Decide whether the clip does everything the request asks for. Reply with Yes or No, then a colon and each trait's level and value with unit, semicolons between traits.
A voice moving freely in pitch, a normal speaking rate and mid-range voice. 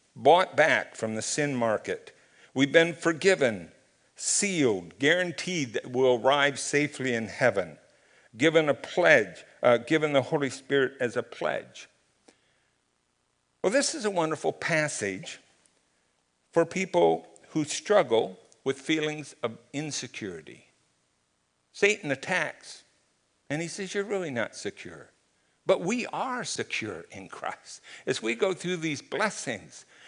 No: wide, 5.7 semitones; slow, 125 wpm; medium, 145 Hz